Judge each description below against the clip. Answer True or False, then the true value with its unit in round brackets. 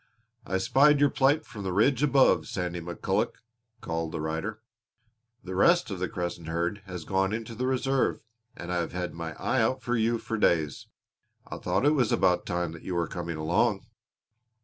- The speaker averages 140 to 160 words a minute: False (195 wpm)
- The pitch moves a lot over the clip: True (6.1 semitones)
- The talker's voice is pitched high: False (95 Hz)